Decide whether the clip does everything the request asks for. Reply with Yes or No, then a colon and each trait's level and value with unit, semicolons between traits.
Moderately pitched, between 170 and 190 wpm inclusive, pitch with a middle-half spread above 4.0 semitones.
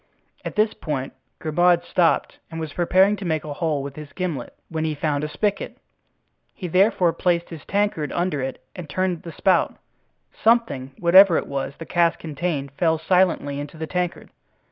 No: medium, 165 Hz; average, 175 wpm; average, 3.4 semitones